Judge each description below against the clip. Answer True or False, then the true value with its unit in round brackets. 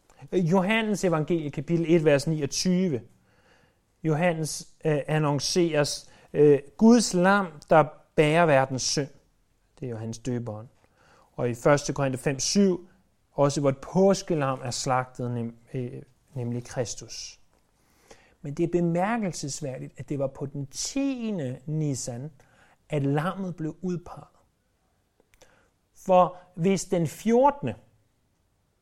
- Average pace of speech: False (115 wpm)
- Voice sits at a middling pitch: True (150 Hz)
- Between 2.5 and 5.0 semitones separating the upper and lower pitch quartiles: False (5.4 semitones)